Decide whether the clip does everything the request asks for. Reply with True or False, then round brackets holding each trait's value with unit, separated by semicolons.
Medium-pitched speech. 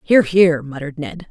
True (160 Hz)